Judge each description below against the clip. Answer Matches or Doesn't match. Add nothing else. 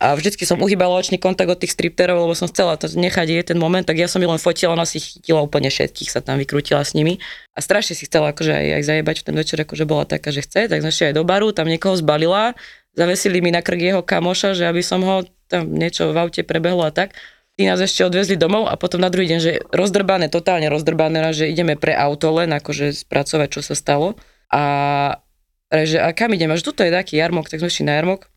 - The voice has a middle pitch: Matches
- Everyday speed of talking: Doesn't match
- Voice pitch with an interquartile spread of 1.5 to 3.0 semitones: Matches